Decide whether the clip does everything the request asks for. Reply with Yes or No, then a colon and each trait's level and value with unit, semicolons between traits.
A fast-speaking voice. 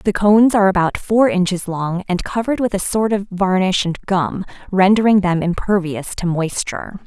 No: average, 180 wpm